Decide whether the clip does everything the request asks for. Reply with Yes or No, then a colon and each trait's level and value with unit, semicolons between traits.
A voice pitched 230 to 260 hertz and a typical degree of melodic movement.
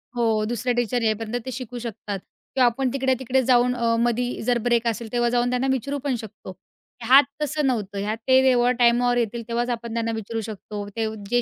No: high, 240 Hz; narrow, 1.8 semitones